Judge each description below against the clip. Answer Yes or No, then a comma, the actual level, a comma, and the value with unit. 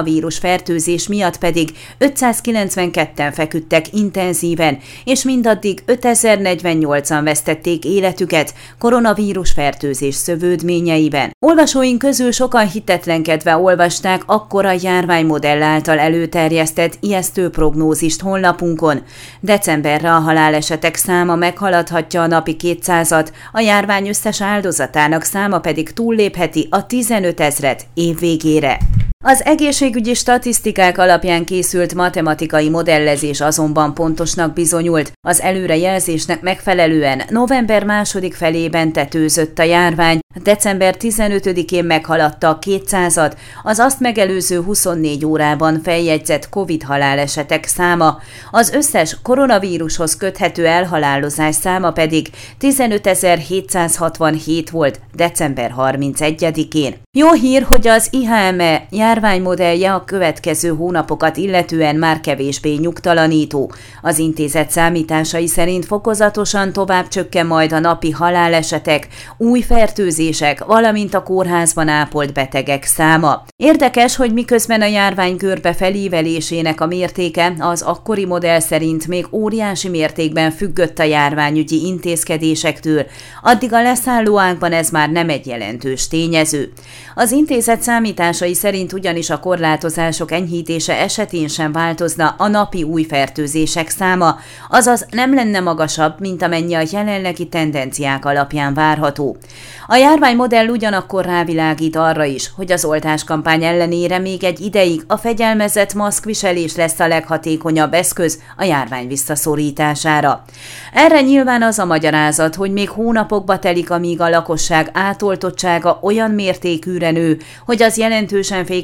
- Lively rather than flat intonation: No, average, 3.8 semitones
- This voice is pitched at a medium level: Yes, medium, 170 Hz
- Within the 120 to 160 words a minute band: No, average, 110 wpm